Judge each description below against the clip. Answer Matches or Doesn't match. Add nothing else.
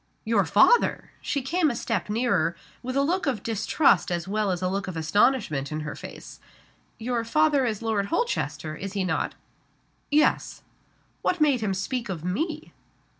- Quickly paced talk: Doesn't match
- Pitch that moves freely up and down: Matches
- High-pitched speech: Matches